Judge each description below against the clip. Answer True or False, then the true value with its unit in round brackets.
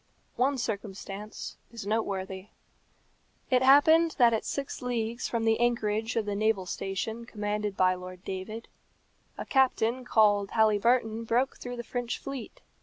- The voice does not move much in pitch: False (3.0 semitones)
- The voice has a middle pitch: False (225 Hz)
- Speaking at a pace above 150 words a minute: False (140 wpm)